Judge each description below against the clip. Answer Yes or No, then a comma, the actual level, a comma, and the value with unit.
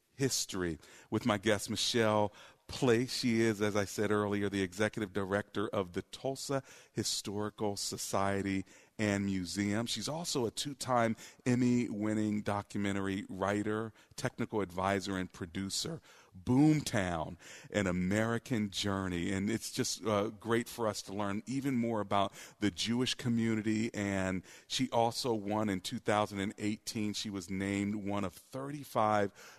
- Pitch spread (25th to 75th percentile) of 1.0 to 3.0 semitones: Yes, average, 2.7 semitones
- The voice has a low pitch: Yes, low, 105 Hz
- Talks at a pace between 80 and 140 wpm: Yes, slow, 135 wpm